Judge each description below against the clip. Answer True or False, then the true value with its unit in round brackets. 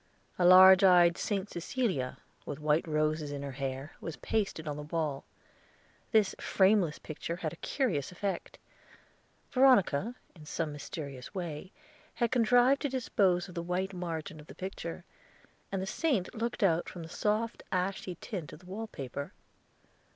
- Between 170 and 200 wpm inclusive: False (155 wpm)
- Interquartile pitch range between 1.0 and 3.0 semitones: False (5.0 semitones)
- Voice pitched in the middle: True (180 Hz)